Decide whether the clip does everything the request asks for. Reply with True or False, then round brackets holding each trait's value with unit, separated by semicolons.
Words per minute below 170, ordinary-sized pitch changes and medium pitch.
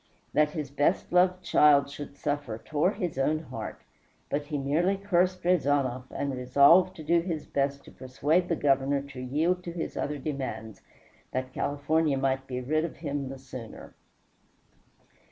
True (160 wpm; 3.6 semitones; 145 Hz)